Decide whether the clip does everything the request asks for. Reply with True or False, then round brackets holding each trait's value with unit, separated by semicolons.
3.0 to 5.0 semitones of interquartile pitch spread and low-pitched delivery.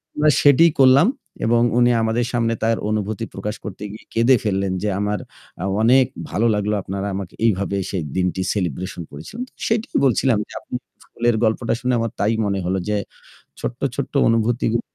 True (3.5 semitones; 110 Hz)